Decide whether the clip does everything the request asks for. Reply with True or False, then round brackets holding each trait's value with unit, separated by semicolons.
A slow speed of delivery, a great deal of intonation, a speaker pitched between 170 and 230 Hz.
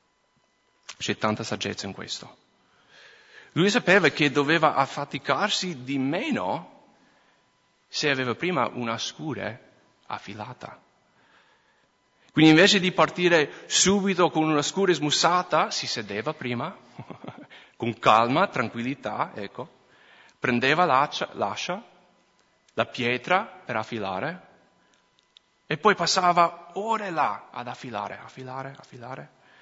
False (105 wpm; 6.2 semitones; 150 Hz)